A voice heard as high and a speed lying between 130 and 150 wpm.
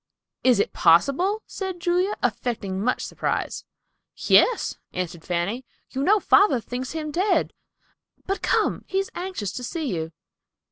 Yes: very high, 265 Hz; average, 140 wpm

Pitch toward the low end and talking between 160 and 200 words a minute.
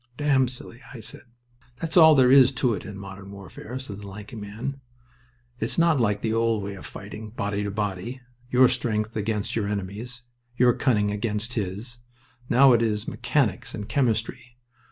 Yes: low, 110 Hz; average, 175 wpm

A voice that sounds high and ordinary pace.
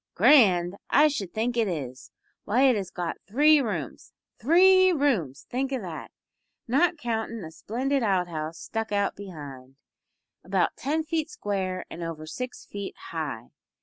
Yes: high, 205 Hz; average, 150 wpm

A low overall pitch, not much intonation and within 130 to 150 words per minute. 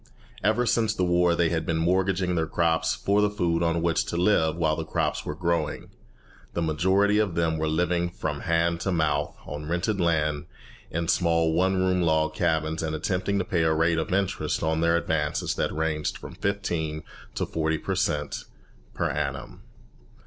No: very low, 85 Hz; narrow, 2.2 semitones; average, 185 wpm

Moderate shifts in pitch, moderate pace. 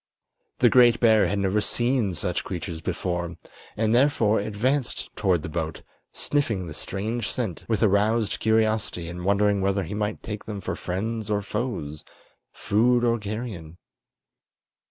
Yes: average, 3.6 semitones; average, 145 wpm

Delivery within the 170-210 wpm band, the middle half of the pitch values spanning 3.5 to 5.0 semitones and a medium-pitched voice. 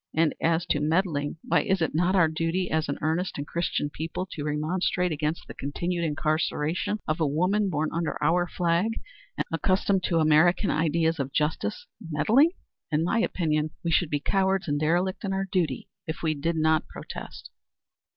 No: average, 180 wpm; average, 3.0 semitones; medium, 165 Hz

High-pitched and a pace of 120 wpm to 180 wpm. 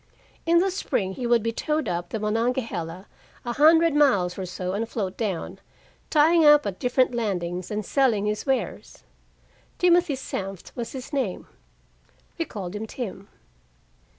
Yes: high, 230 Hz; average, 150 wpm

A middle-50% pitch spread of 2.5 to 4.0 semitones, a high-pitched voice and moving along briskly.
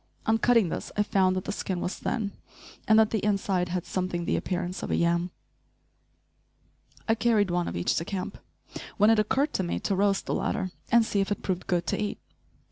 Yes: average, 2.9 semitones; high, 195 Hz; fast, 210 wpm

